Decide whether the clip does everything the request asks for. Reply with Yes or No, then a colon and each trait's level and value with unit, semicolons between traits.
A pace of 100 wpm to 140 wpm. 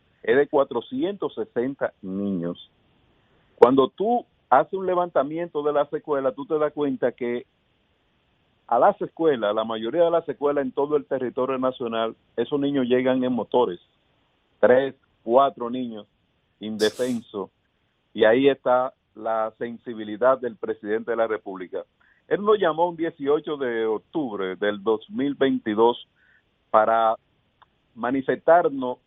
Yes: slow, 125 wpm